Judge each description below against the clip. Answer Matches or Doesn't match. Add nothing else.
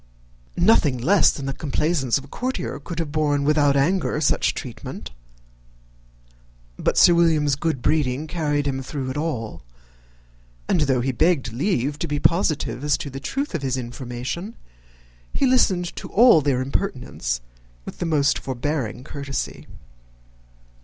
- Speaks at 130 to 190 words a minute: Matches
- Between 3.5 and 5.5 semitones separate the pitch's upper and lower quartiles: Matches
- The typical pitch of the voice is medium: Matches